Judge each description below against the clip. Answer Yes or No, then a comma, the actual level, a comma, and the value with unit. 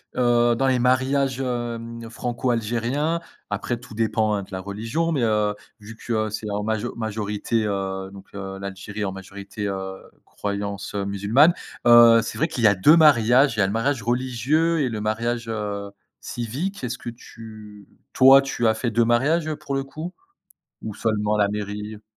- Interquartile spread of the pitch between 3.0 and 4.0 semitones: Yes, average, 3.5 semitones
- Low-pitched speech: Yes, low, 115 Hz